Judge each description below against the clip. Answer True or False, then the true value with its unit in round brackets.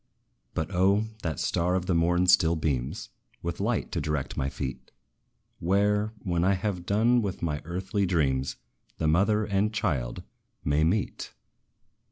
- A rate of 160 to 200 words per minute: False (150 wpm)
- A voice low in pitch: True (90 Hz)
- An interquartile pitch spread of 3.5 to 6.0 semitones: True (4.1 semitones)